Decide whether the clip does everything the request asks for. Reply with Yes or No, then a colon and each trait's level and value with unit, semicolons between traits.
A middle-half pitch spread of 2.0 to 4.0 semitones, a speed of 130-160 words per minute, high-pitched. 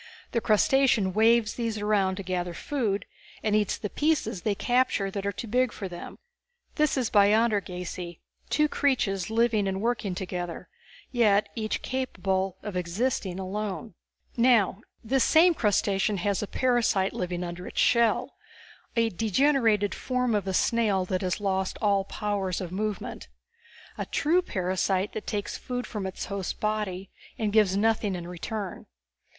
Yes: average, 3.5 semitones; average, 150 wpm; high, 205 Hz